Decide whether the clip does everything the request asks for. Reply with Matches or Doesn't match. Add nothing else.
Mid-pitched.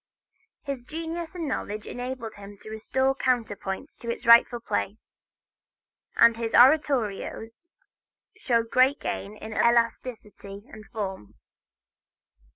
Doesn't match